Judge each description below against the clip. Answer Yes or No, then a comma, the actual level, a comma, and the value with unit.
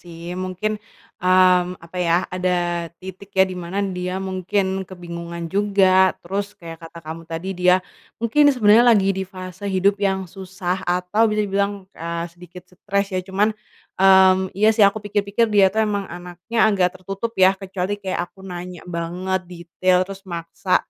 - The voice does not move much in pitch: Yes, narrow, 1.8 semitones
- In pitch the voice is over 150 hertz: Yes, high, 190 Hz